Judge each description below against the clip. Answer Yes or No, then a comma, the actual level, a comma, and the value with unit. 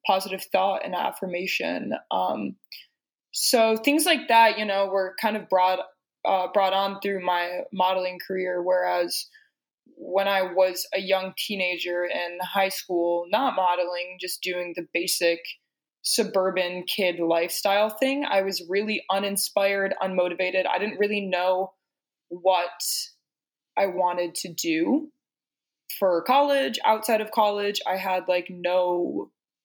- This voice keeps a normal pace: No, slow, 130 wpm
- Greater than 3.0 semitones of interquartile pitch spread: No, narrow, 2.5 semitones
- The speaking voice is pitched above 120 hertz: Yes, high, 190 Hz